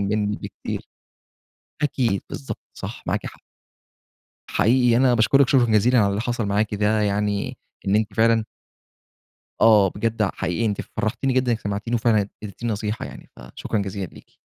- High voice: No, low, 110 Hz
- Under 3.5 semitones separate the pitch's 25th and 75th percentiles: Yes, narrow, 2.4 semitones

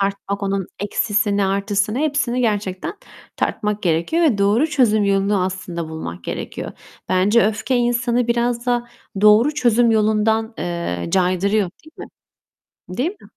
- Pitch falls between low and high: No, high, 210 Hz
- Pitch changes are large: No, average, 3.5 semitones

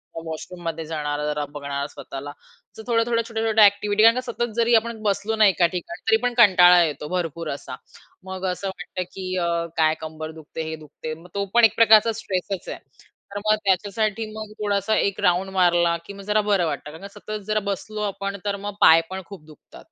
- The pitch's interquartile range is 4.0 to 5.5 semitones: Yes, average, 4.7 semitones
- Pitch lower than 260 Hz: Yes, high, 190 Hz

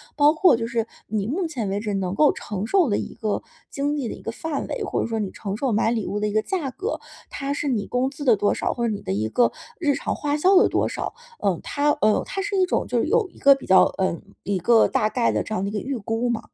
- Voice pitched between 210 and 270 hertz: Yes, high, 235 Hz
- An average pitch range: No, wide, 5.8 semitones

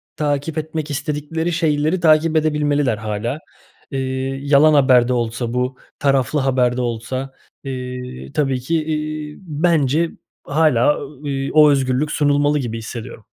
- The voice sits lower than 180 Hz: Yes, medium, 140 Hz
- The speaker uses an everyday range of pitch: Yes, average, 3.2 semitones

